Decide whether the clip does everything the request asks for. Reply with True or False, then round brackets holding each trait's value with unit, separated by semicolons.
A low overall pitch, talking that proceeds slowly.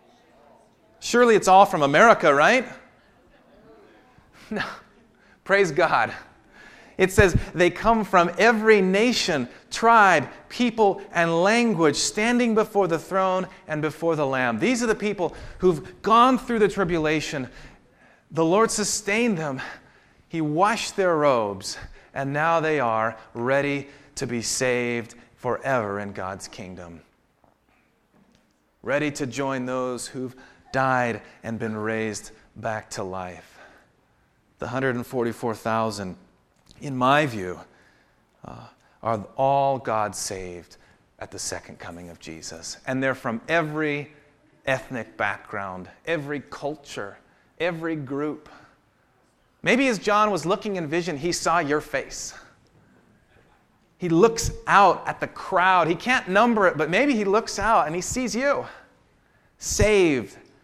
False (150 Hz; 125 wpm)